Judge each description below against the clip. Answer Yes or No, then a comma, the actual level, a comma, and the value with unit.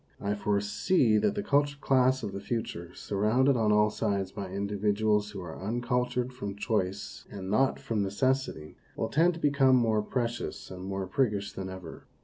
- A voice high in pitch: No, low, 105 Hz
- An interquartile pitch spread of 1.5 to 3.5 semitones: No, average, 4.3 semitones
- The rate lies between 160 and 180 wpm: Yes, average, 170 wpm